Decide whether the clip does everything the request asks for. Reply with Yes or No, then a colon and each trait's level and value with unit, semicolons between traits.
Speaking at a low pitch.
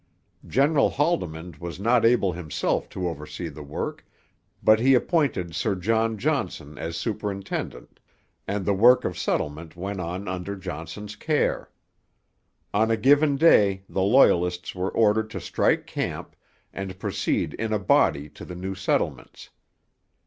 Yes: low, 100 Hz